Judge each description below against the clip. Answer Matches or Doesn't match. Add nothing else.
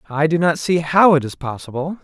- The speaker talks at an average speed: Doesn't match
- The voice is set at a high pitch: Doesn't match